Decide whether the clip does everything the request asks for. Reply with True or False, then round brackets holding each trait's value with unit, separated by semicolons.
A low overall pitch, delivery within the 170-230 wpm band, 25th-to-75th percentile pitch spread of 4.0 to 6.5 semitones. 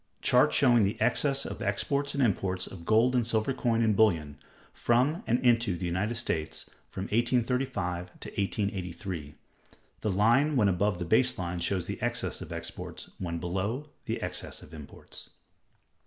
False (105 Hz; 160 wpm; 5.2 semitones)